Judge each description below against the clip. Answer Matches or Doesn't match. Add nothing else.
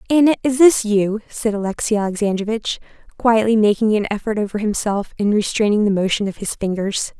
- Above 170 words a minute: Doesn't match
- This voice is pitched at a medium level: Doesn't match